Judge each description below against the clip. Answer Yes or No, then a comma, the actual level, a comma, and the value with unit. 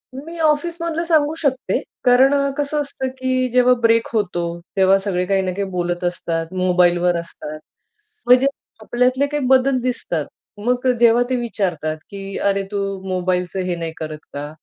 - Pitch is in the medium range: No, high, 215 Hz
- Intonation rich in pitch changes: Yes, wide, 6.5 semitones